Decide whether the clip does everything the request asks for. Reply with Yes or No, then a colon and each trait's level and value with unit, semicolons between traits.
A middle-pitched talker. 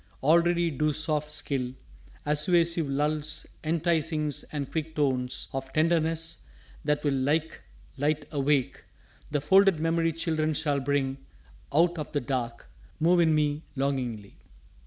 Yes: medium, 150 Hz